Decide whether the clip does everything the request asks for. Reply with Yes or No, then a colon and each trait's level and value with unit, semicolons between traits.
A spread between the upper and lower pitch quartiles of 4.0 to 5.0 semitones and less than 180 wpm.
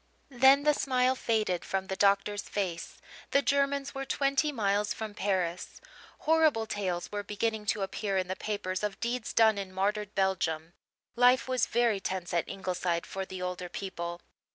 Yes: average, 4.4 semitones; average, 165 wpm